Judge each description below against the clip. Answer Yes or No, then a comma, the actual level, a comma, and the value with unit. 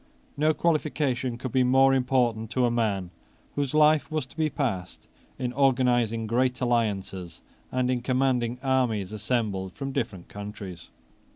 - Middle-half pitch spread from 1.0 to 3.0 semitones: No, average, 3.5 semitones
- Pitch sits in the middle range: No, low, 125 Hz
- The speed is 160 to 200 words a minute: No, average, 145 wpm